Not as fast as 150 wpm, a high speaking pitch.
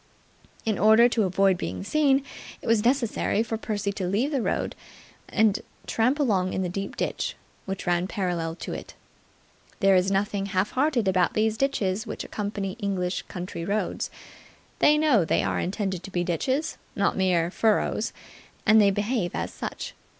No: average, 165 wpm; high, 200 Hz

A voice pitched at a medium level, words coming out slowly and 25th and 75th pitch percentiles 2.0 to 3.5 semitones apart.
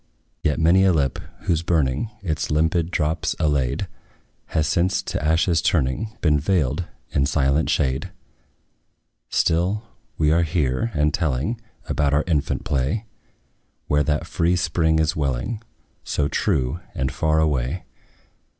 No: very low, 80 Hz; slow, 130 wpm; average, 3.1 semitones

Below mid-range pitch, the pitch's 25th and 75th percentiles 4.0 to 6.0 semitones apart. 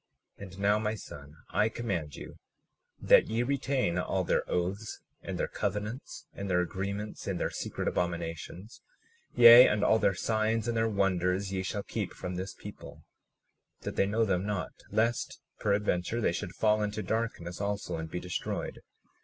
No: low, 100 Hz; average, 3.4 semitones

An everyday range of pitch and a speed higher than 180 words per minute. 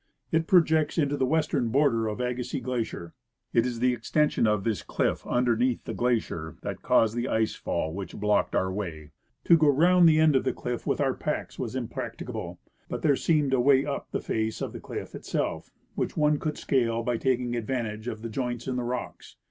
Yes: average, 4.2 semitones; fast, 205 wpm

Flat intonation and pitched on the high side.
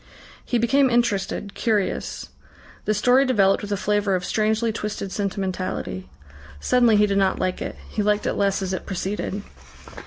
Yes: narrow, 2.3 semitones; high, 205 Hz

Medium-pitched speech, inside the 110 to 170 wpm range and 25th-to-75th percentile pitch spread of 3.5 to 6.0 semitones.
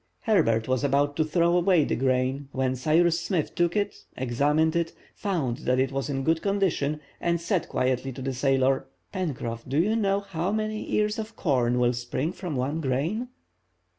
No: medium, 150 Hz; average, 180 wpm; average, 5.2 semitones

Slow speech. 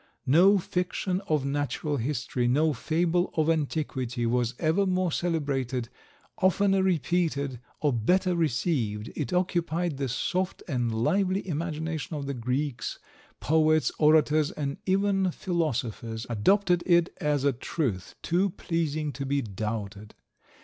Yes: slow, 125 wpm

